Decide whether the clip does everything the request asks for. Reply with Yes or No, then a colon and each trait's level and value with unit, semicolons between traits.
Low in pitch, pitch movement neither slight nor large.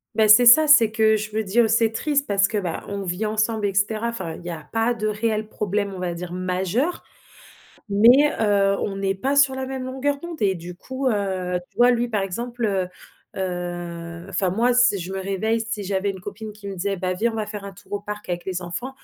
No: high, 205 Hz; average, 3.6 semitones